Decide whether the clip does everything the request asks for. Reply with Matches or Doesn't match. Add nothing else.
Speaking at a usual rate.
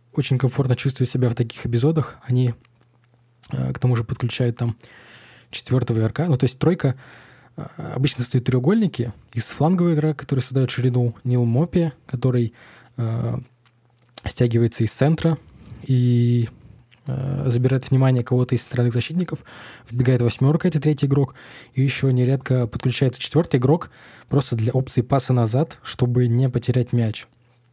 Matches